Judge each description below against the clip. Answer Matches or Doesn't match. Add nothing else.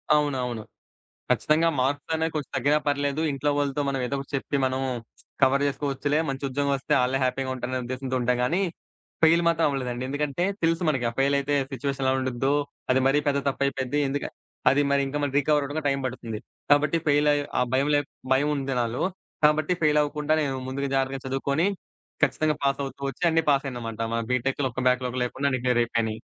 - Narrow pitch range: Matches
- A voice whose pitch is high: Doesn't match